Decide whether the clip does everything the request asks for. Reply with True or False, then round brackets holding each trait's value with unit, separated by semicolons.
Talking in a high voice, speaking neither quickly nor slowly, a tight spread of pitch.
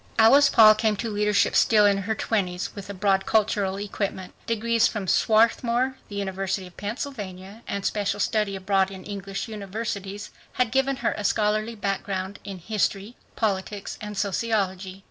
True (205 Hz; 160 wpm; 2.2 semitones)